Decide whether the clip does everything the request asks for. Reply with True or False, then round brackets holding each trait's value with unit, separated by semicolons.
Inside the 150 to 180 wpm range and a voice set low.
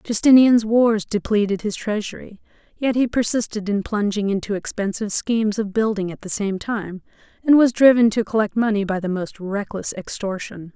False (165 wpm; 210 Hz)